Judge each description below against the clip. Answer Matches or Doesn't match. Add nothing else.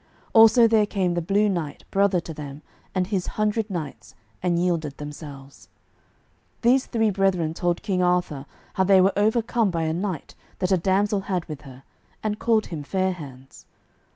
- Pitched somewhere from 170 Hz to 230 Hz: Matches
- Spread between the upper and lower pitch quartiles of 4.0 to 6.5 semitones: Matches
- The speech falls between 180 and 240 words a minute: Doesn't match